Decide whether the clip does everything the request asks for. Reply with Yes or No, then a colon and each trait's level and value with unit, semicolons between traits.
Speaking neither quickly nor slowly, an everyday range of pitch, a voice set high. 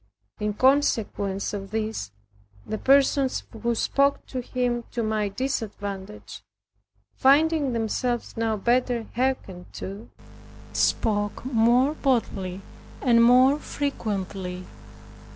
No: slow, 100 wpm; average, 4.2 semitones; high, 230 Hz